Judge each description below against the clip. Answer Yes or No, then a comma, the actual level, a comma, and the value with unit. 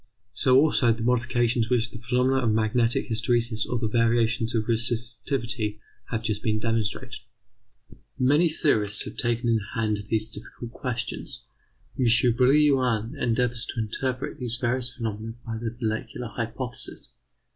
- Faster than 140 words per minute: No, slow, 135 wpm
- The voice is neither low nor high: No, low, 115 Hz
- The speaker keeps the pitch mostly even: Yes, narrow, 1.9 semitones